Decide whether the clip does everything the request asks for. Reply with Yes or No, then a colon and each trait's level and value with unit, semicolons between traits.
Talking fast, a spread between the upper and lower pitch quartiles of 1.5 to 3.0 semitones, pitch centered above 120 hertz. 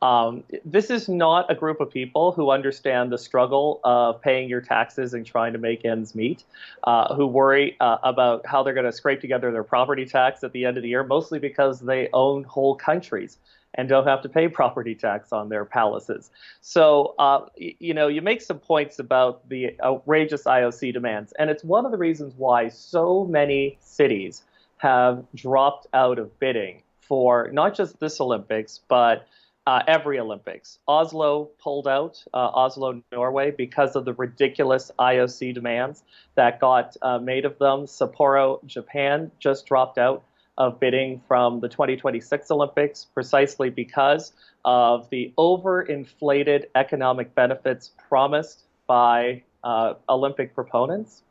No: average, 160 wpm; narrow, 2.6 semitones; low, 135 Hz